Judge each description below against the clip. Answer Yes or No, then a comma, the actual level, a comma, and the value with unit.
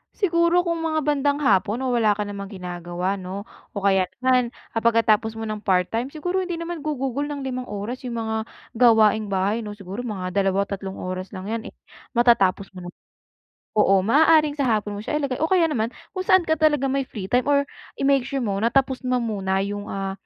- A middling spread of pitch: No, wide, 6.0 semitones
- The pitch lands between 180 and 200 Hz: No, high, 230 Hz